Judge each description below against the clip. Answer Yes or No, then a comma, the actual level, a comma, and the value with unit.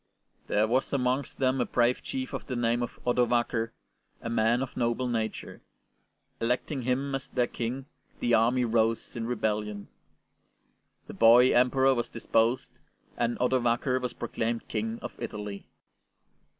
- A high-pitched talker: No, low, 120 Hz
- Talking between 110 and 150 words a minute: Yes, average, 140 wpm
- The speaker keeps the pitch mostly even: Yes, narrow, 1.9 semitones